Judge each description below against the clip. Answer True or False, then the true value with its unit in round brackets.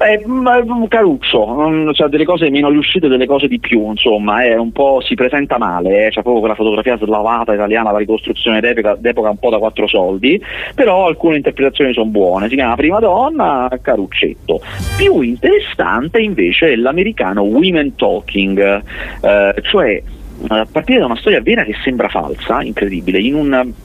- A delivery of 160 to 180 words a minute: True (170 wpm)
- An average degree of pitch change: False (6.2 semitones)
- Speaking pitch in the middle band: False (125 Hz)